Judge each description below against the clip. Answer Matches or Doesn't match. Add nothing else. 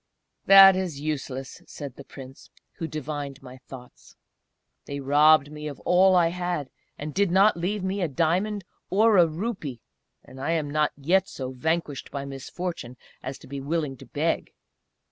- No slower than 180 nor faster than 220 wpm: Doesn't match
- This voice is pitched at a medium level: Matches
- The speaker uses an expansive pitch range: Doesn't match